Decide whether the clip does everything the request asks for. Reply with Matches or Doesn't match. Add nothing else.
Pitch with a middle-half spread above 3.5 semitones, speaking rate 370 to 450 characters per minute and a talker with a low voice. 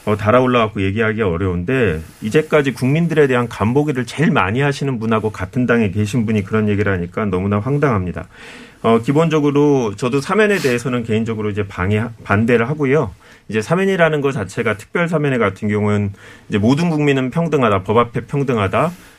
Matches